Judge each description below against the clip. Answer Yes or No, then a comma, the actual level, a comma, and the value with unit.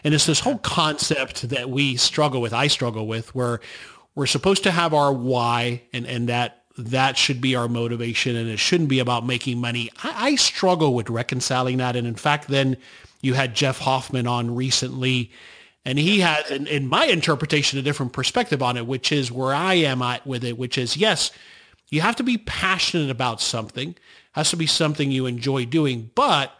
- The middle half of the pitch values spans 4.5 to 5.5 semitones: No, average, 3.5 semitones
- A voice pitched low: Yes, low, 130 Hz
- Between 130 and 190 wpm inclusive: No, average, 200 wpm